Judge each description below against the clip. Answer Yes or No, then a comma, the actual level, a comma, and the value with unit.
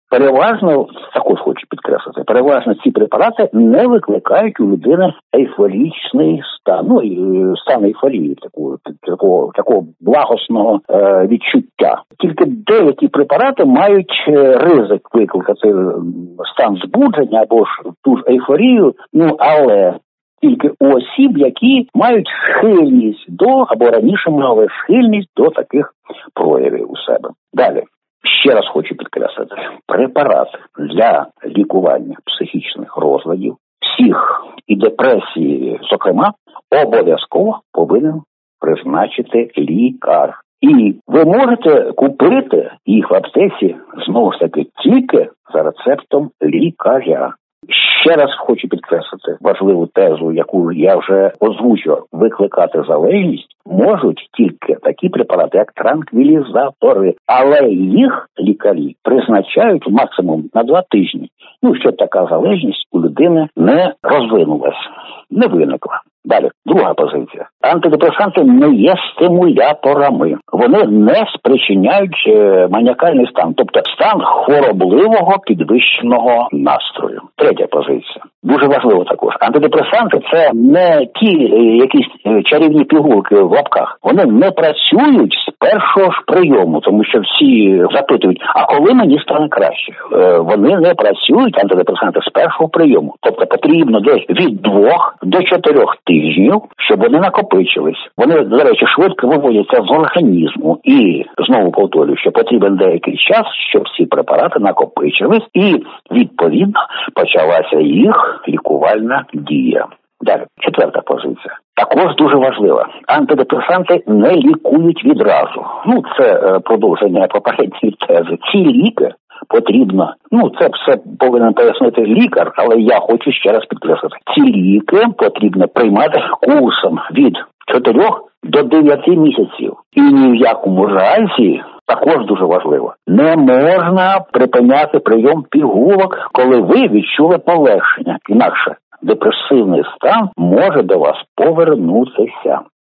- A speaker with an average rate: Yes, average, 115 wpm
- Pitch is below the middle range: No, very high, 290 Hz